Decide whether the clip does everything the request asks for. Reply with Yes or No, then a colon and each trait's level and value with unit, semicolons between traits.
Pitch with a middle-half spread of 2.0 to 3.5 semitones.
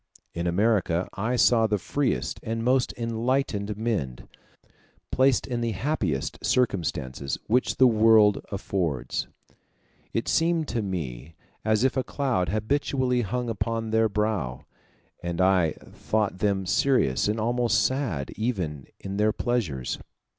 No: average, 5.0 semitones